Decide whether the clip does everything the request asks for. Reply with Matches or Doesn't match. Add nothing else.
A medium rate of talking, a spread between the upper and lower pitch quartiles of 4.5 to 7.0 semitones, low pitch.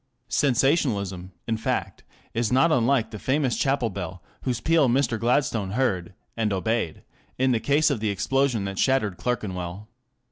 Matches